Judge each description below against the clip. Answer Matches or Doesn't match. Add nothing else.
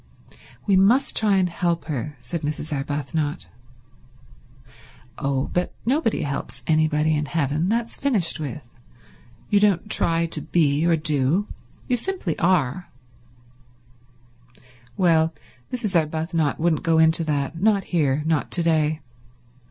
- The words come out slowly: Matches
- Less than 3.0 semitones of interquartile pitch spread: Doesn't match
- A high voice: Doesn't match